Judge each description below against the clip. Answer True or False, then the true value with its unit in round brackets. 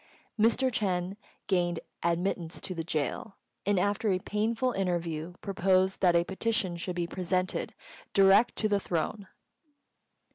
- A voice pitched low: False (185 Hz)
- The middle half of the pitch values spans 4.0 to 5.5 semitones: False (2.7 semitones)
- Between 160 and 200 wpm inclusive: False (135 wpm)